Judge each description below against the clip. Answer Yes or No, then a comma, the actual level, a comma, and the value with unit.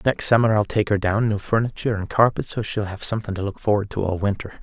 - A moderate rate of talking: No, fast, 260 wpm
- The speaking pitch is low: Yes, low, 105 Hz